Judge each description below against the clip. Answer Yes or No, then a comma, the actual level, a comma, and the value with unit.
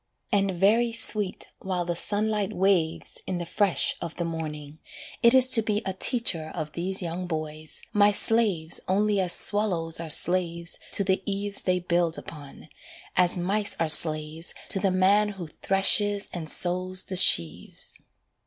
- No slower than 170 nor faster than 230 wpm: No, average, 160 wpm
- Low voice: No, medium, 185 Hz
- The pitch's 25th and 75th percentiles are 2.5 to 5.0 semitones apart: Yes, average, 3.6 semitones